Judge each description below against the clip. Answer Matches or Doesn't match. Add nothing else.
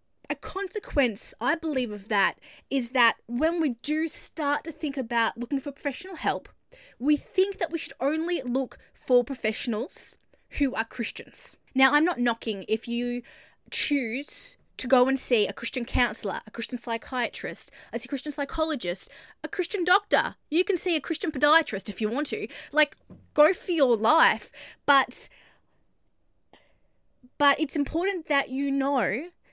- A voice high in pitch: Matches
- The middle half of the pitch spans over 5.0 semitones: Doesn't match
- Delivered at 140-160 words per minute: Matches